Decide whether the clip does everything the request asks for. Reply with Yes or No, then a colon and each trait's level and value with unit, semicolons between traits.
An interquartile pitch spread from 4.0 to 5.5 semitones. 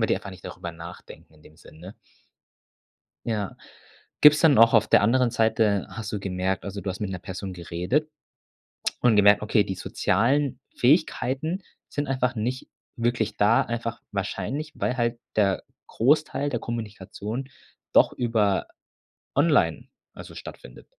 Yes: average, 4.6 semitones